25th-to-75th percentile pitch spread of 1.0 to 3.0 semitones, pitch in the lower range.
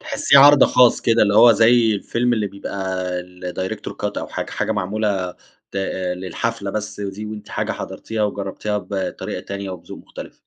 Yes: average, 2.7 semitones; low, 105 Hz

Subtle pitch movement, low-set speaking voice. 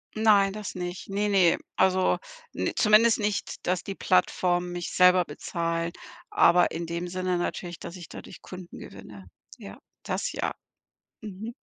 No: narrow, 2.3 semitones; medium, 180 Hz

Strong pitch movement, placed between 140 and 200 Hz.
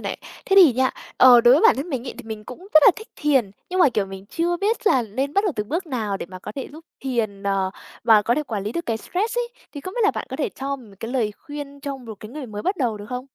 No: wide, 6.1 semitones; very high, 260 Hz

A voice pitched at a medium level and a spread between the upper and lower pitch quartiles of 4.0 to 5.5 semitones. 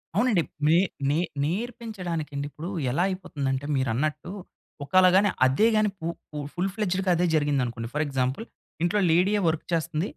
Yes: medium, 165 Hz; average, 4.9 semitones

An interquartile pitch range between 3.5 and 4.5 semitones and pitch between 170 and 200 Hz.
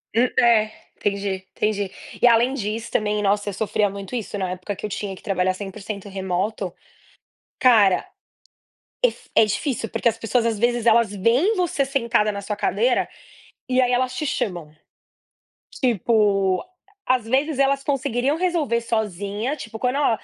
No: average, 3.8 semitones; high, 220 Hz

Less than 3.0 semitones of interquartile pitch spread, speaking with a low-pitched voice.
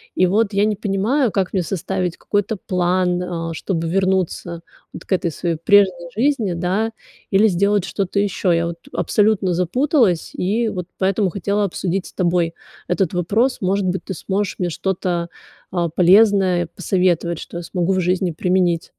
No: narrow, 2.4 semitones; medium, 185 Hz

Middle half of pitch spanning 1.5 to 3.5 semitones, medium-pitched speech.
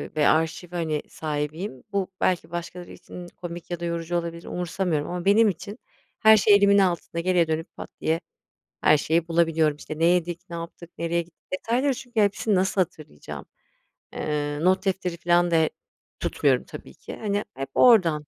Yes: average, 2.7 semitones; medium, 175 Hz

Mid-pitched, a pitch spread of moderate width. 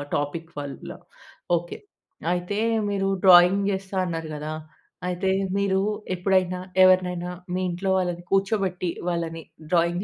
No: medium, 180 Hz; narrow, 1.8 semitones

